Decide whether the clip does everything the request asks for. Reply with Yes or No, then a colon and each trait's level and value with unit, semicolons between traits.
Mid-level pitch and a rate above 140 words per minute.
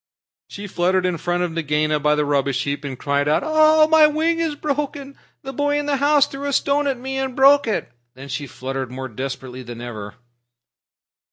Yes: medium, 180 Hz; average, 200 wpm